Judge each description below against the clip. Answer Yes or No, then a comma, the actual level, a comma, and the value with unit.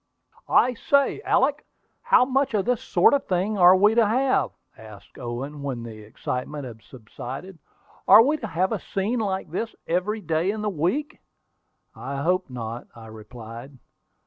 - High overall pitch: No, medium, 180 Hz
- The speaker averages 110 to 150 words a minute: No, average, 170 wpm